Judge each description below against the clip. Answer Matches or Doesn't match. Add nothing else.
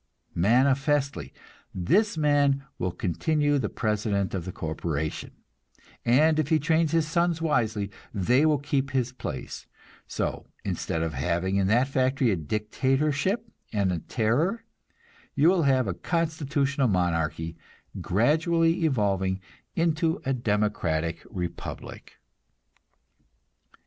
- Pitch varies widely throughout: Matches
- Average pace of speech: Doesn't match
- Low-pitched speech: Matches